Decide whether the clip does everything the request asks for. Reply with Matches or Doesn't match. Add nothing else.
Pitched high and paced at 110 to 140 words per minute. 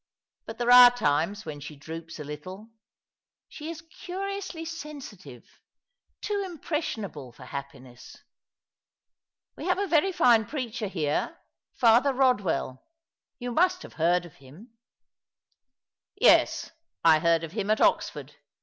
Matches